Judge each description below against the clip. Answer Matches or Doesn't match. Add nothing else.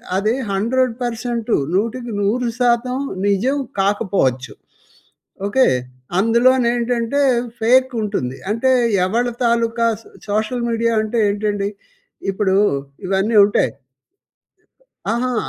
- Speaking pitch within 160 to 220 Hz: Doesn't match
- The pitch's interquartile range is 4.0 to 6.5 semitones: Doesn't match